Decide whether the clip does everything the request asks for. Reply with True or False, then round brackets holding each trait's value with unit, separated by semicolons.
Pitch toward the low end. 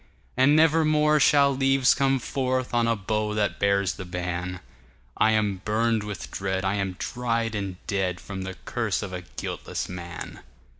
True (105 Hz)